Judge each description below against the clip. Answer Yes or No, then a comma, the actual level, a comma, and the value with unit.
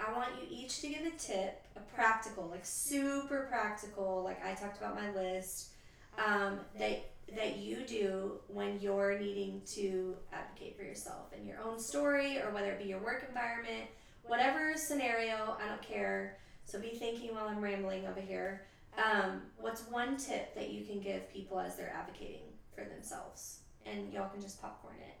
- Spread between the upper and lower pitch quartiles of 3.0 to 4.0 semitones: Yes, average, 3.5 semitones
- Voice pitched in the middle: No, high, 205 Hz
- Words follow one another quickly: No, average, 180 wpm